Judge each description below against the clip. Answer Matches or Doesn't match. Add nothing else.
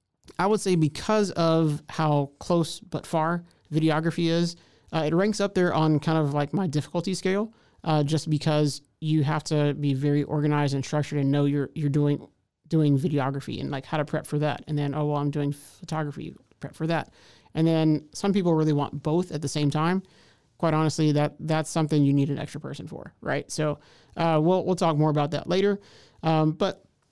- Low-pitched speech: Doesn't match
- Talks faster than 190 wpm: Matches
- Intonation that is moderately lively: Doesn't match